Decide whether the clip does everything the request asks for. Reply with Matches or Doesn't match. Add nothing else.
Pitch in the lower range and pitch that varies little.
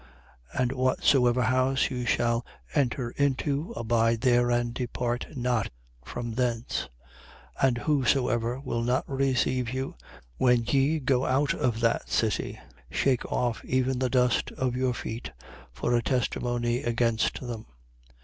Matches